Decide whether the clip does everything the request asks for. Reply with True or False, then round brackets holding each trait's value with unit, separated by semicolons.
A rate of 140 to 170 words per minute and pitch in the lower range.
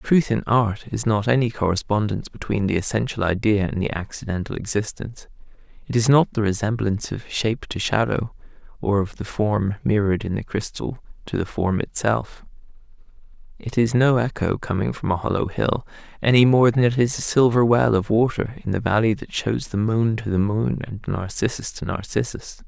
False (185 wpm; 110 Hz)